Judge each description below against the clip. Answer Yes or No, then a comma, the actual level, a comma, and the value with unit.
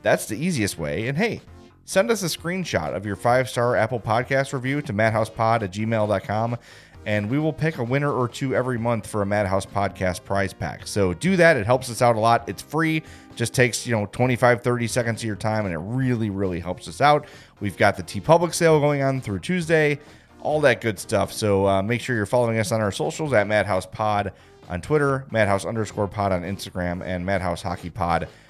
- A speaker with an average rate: No, fast, 210 wpm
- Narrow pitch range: No, average, 4.7 semitones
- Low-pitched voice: Yes, low, 110 Hz